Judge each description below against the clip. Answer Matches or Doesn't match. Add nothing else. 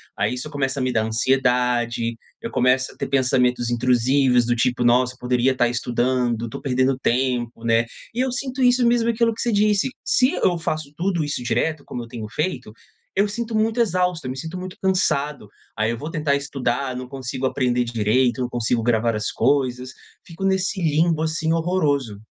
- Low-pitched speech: Matches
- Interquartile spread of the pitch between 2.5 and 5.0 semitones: Doesn't match